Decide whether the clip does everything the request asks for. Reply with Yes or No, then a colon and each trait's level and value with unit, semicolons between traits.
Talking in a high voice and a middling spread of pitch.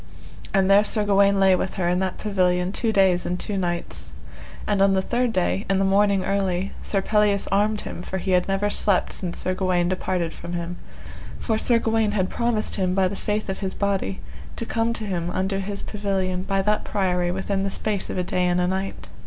No: high, 195 Hz; narrow, 2.0 semitones